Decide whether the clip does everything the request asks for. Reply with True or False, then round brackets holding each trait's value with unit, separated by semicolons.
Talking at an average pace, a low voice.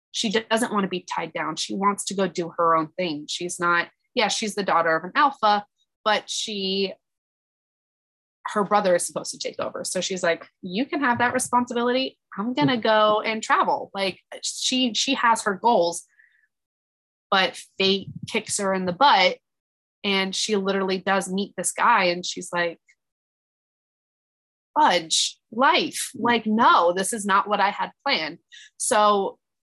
False (165 wpm; 200 Hz)